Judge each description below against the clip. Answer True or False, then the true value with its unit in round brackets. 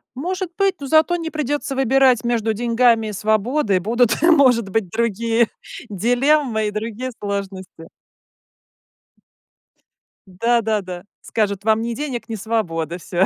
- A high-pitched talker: True (230 Hz)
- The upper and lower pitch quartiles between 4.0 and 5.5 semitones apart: True (4.3 semitones)